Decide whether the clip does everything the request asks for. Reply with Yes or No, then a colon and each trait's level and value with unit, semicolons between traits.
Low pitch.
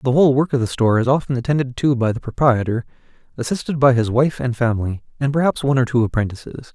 Yes: low, 130 Hz